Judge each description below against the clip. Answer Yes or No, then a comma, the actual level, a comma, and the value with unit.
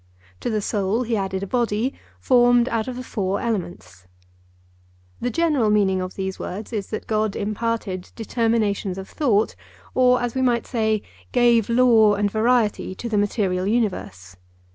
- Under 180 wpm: Yes, average, 160 wpm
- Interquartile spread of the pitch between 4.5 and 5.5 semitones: No, average, 3.3 semitones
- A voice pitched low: No, high, 220 Hz